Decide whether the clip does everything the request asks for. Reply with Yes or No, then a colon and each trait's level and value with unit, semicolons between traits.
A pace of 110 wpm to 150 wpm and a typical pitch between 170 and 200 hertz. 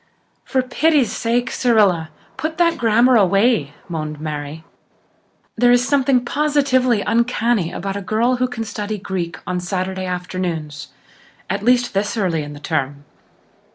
No: average, 140 wpm; high, 210 Hz